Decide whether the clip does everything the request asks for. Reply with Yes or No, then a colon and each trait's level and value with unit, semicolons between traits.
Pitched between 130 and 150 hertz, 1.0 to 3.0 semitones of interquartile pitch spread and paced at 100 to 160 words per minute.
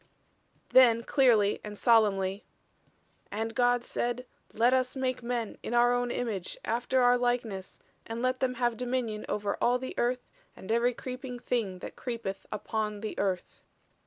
No: high, 240 Hz; narrow, 2.6 semitones; average, 150 wpm